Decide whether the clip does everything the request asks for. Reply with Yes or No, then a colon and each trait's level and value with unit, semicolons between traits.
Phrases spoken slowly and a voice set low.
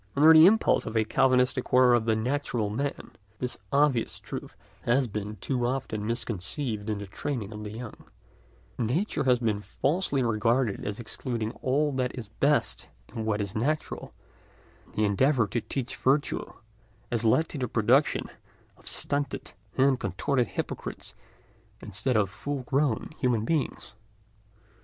No: average, 150 wpm; low, 125 Hz